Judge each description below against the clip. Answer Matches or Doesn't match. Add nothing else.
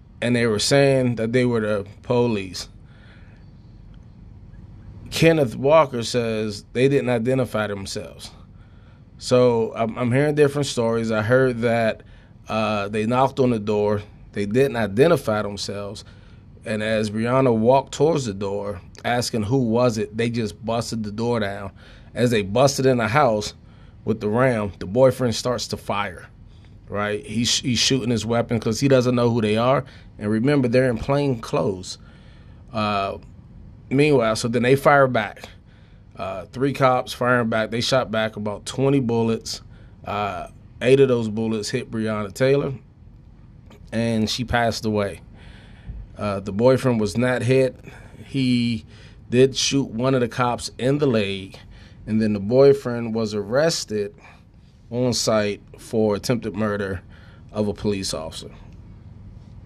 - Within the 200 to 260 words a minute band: Doesn't match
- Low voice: Matches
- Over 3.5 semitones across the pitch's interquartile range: Doesn't match